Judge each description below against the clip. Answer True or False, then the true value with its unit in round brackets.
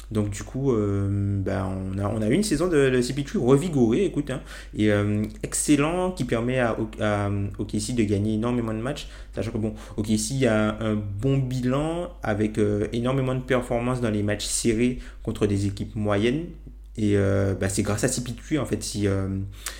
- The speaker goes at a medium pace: True (190 wpm)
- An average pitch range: True (3.7 semitones)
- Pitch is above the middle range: False (110 Hz)